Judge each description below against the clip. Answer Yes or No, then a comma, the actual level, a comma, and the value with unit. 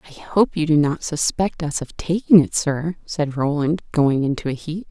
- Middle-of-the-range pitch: Yes, medium, 155 Hz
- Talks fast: Yes, fast, 210 wpm